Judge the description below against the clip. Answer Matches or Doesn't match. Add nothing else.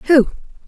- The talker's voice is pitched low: Doesn't match